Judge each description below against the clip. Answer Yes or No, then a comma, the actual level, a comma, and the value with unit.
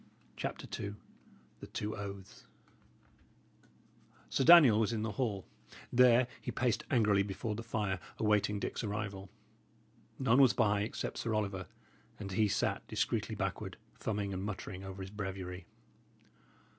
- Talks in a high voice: No, low, 105 Hz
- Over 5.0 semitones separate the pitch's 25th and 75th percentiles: No, narrow, 2.5 semitones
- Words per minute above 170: No, slow, 135 wpm